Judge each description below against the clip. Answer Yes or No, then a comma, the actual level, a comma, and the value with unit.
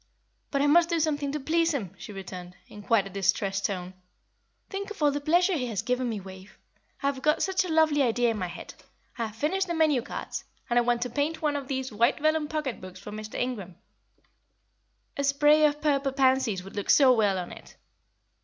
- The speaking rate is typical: No, fast, 220 wpm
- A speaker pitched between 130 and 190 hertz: No, very high, 265 Hz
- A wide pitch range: Yes, wide, 6.4 semitones